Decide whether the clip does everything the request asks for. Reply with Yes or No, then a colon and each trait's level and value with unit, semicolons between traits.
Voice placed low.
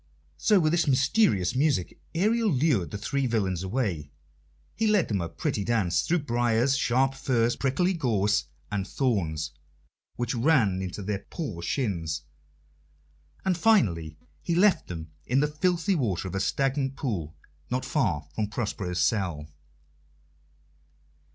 Yes: low, 120 Hz